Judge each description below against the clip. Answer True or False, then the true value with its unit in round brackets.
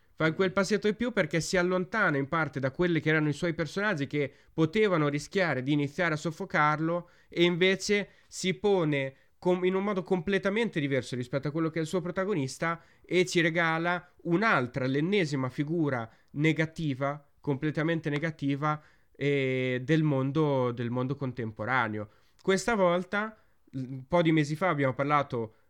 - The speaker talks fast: False (155 wpm)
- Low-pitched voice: False (160 Hz)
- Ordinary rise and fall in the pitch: True (4.5 semitones)